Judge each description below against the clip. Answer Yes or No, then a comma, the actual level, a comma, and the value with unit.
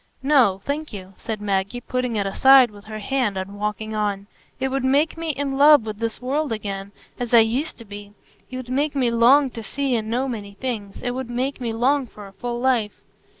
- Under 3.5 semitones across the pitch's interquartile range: No, average, 4.2 semitones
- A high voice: Yes, high, 240 Hz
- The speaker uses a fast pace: Yes, fast, 220 wpm